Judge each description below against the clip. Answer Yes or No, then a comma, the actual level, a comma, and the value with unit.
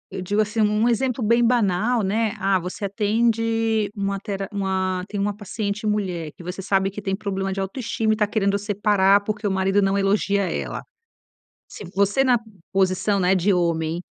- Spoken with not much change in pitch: Yes, narrow, 2.0 semitones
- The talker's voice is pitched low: No, high, 200 Hz